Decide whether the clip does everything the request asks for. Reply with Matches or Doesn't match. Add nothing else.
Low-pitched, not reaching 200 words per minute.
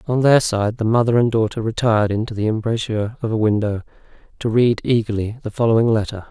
Matches